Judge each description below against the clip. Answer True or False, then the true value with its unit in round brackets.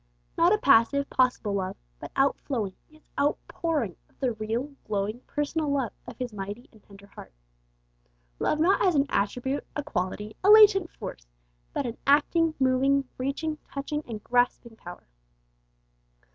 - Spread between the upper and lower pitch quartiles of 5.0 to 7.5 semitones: True (5.6 semitones)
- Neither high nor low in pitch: False (260 Hz)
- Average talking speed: True (145 wpm)